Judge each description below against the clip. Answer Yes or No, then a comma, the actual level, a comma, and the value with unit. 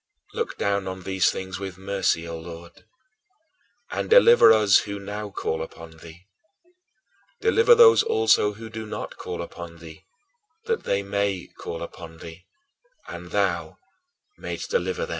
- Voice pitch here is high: No, very low, 95 Hz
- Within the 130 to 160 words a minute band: Yes, average, 140 wpm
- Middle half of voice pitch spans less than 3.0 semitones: No, average, 4.5 semitones